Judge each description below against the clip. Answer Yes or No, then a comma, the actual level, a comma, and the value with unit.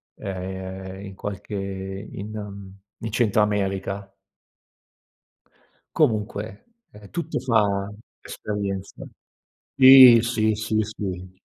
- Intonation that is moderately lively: No, narrow, 2.0 semitones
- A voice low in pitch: Yes, low, 100 Hz